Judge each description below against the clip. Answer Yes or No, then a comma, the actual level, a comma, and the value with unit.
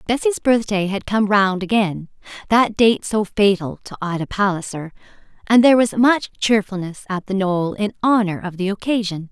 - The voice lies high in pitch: Yes, high, 205 Hz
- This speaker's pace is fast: No, average, 155 wpm